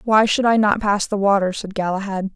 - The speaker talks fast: Yes, fast, 230 wpm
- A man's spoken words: No, female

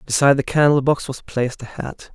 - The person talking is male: Yes, male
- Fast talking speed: Yes, fast, 225 wpm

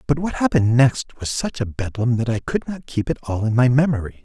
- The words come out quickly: Yes, fast, 255 wpm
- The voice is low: Yes, low, 125 Hz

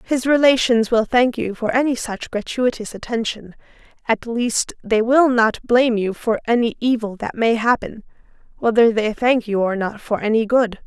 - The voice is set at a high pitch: Yes, high, 230 Hz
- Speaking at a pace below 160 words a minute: No, average, 175 wpm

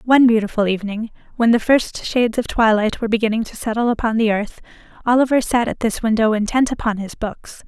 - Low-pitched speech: No, high, 225 Hz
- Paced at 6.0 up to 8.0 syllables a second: Yes, 6.1 syllables/s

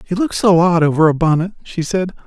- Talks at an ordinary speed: No, fast, 240 wpm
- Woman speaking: No, male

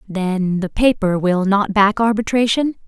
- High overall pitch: Yes, high, 205 Hz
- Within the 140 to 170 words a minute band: Yes, average, 145 wpm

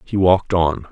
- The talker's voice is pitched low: Yes, very low, 85 Hz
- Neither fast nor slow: Yes, average, 195 wpm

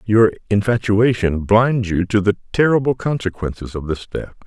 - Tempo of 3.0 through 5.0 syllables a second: Yes, 4.7 syllables/s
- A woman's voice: No, male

